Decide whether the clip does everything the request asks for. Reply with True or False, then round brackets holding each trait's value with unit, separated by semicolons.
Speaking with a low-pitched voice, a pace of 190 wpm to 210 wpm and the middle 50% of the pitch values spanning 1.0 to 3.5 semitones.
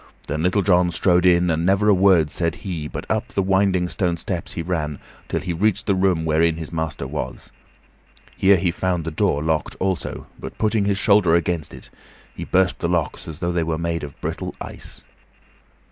True (85 Hz; 200 wpm; 2.6 semitones)